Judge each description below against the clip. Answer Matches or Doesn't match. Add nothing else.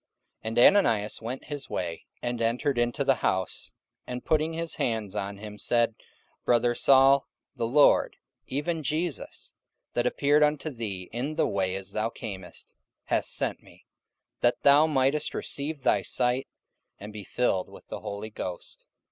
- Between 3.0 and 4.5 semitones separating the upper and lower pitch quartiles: Doesn't match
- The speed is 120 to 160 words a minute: Matches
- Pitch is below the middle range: Matches